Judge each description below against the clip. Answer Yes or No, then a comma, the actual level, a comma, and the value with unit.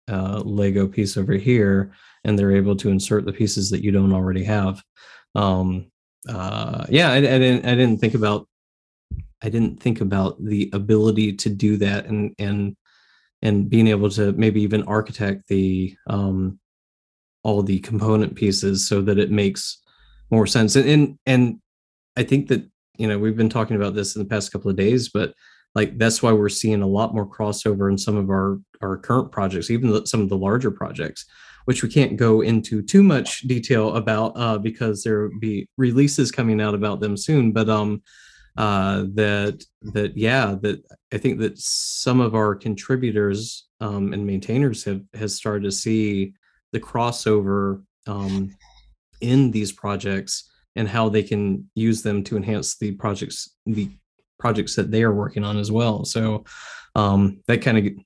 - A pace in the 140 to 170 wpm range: No, average, 180 wpm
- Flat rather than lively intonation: Yes, narrow, 2.1 semitones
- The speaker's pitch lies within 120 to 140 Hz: No, low, 105 Hz